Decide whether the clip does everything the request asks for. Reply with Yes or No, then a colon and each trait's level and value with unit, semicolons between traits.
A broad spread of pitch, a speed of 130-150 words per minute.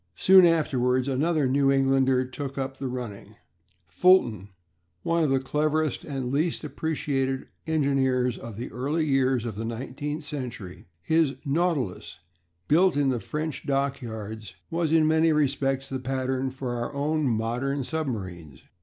No: average, 3.3 semitones; average, 140 wpm